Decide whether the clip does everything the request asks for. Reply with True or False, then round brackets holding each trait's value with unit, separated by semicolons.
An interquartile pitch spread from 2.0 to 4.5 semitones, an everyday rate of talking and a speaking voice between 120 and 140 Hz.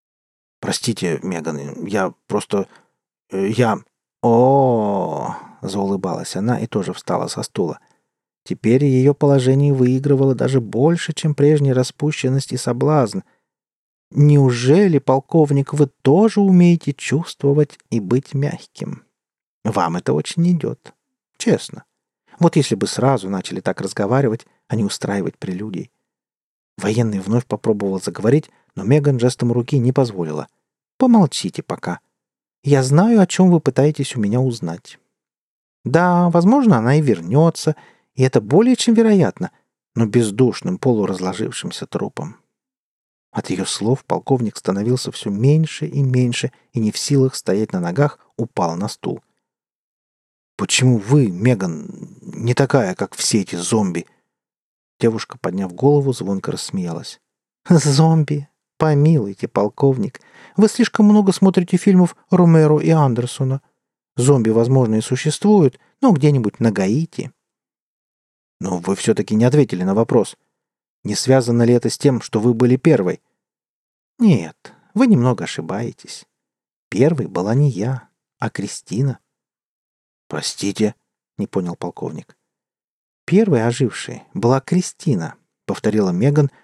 False (5.4 semitones; 120 wpm; 135 Hz)